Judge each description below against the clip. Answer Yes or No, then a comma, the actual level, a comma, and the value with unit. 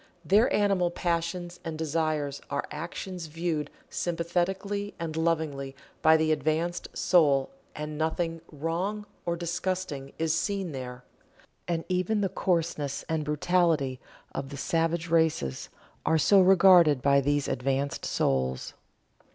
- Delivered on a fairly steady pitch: No, average, 3.2 semitones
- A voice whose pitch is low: No, medium, 165 Hz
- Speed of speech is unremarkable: No, slow, 125 wpm